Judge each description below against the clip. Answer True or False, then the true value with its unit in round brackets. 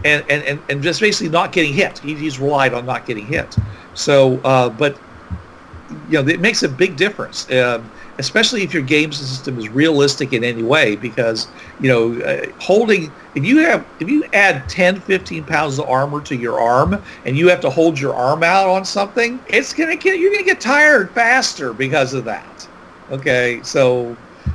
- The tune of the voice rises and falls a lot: True (7.2 semitones)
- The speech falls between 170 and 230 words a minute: True (195 wpm)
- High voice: False (150 Hz)